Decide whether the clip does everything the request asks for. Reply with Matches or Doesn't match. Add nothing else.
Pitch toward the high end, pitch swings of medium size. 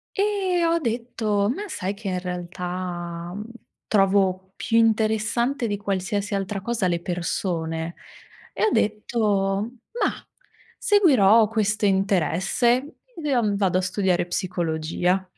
Matches